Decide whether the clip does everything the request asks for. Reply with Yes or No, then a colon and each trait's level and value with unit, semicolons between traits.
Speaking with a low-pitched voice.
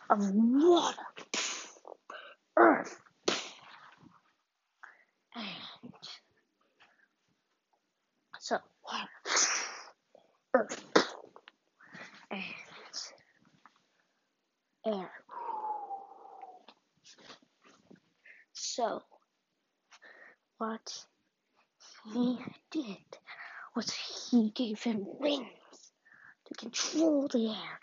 No: very high, 285 Hz